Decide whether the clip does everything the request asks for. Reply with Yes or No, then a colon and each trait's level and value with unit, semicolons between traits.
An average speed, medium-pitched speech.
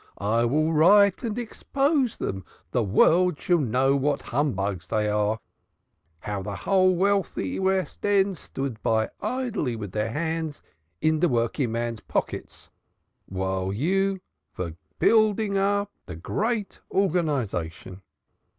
No: slow, 125 wpm; medium, 150 Hz